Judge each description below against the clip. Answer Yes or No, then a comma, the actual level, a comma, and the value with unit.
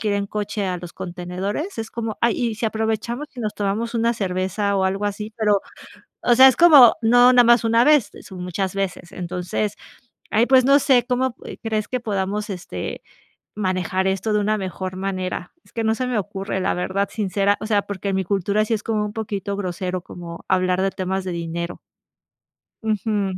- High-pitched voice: Yes, high, 205 Hz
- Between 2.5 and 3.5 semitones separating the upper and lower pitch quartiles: Yes, average, 3.1 semitones